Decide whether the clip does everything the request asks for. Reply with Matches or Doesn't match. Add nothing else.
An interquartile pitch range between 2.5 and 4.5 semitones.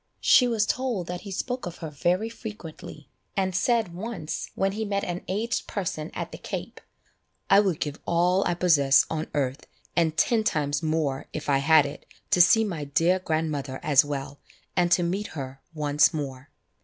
Doesn't match